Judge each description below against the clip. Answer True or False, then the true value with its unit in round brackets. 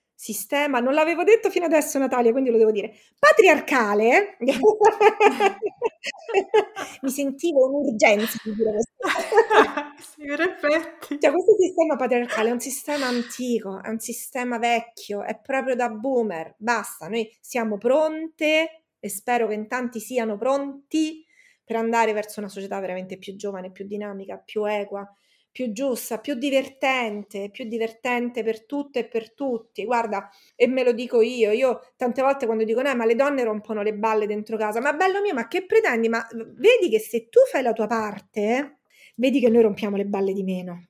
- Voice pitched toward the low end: False (245 Hz)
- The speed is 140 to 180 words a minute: True (160 wpm)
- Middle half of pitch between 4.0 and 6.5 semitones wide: True (5.0 semitones)